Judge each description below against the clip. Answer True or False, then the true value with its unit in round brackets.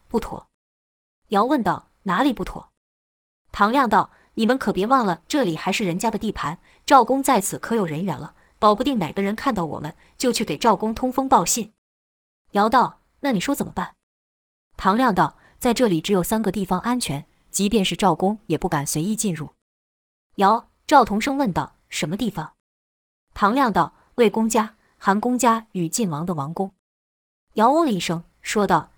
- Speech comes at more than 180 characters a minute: True (255 characters per minute)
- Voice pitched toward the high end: True (195 Hz)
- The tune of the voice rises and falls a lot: True (5.9 semitones)